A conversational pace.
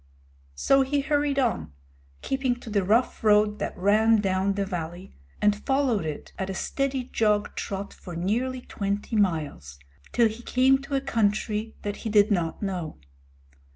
Yes: average, 160 wpm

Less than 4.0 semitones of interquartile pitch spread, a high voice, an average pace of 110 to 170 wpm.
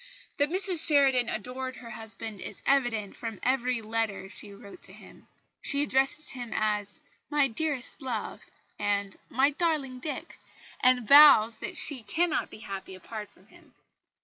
No: average, 4.6 semitones; very high, 250 Hz; average, 150 wpm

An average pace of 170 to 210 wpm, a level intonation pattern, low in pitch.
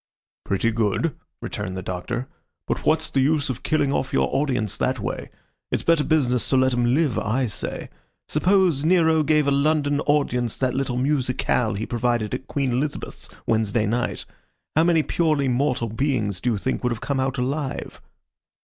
No: average, 175 wpm; average, 3.8 semitones; low, 130 Hz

